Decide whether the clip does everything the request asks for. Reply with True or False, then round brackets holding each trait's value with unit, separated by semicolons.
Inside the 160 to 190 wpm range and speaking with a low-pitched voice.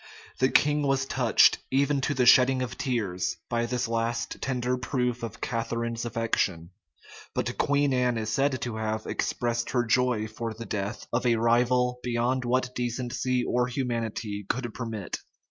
True (165 wpm; 120 Hz)